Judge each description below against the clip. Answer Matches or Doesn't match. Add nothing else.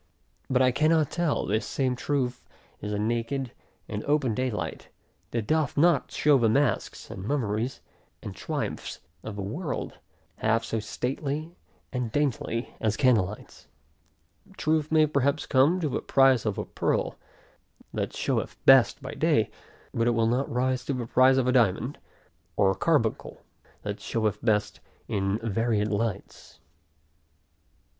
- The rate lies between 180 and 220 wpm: Doesn't match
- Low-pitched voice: Matches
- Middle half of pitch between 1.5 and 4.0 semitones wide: Doesn't match